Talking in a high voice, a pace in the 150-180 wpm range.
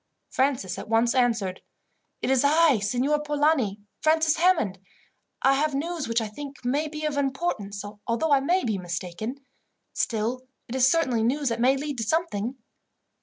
Yes: very high, 265 Hz; average, 165 wpm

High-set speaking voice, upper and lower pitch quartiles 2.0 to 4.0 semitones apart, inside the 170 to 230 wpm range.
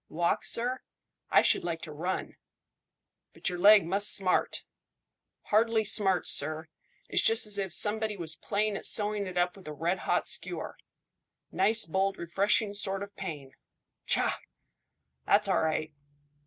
No: high, 195 Hz; average, 3.5 semitones; average, 150 wpm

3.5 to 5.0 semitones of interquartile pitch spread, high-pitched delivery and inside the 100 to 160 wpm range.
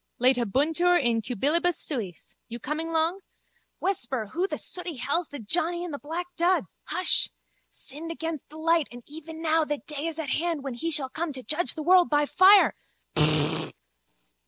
No: average, 3.9 semitones; very high, 315 Hz; average, 170 wpm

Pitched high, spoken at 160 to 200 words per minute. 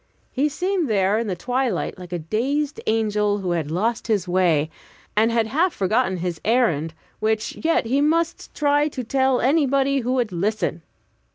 Yes: high, 225 Hz; average, 175 wpm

